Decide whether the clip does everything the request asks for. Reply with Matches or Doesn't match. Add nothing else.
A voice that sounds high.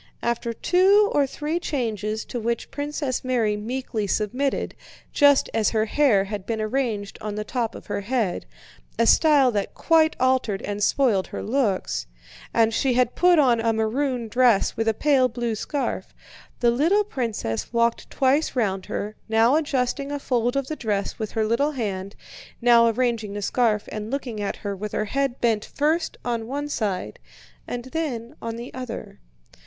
Matches